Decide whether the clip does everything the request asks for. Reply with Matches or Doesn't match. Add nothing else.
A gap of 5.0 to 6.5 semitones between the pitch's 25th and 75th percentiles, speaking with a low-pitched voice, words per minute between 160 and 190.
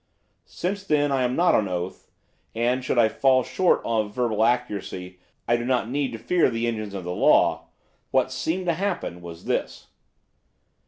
Matches